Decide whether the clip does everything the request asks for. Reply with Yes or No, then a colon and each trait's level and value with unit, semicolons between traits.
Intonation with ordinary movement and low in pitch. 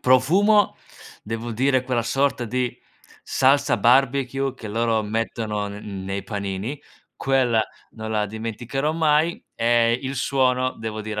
Yes: average, 3.6 semitones; low, 120 Hz